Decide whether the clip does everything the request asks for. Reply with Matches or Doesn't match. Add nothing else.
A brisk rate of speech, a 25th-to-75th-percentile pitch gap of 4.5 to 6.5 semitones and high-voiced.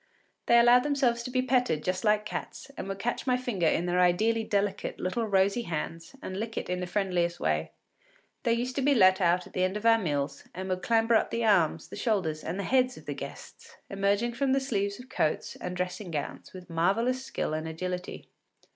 Matches